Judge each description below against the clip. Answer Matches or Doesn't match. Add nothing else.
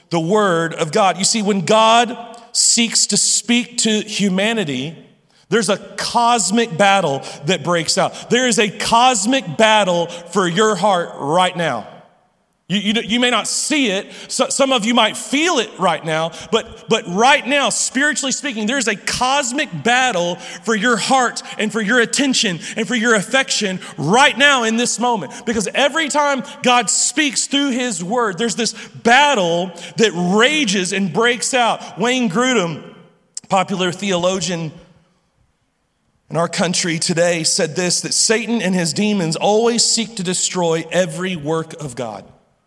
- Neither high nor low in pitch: Doesn't match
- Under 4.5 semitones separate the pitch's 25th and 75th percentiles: Doesn't match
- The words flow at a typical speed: Matches